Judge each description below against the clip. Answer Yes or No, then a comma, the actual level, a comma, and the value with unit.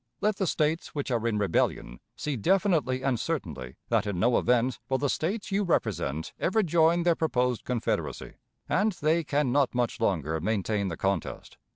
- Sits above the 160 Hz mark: No, low, 130 Hz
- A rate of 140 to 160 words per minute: No, average, 175 wpm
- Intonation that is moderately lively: No, wide, 7.7 semitones